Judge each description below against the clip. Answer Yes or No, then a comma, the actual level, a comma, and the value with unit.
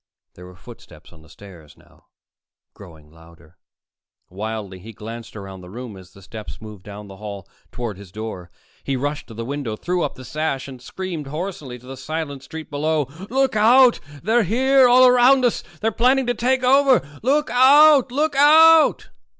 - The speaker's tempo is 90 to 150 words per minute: No, average, 180 wpm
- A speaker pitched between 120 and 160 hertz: Yes, medium, 140 Hz